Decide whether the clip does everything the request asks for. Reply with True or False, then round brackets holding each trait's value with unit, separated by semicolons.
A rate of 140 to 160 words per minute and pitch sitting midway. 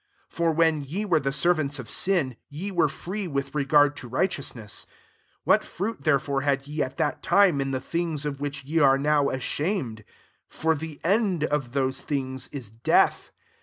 False (175 wpm; 145 Hz)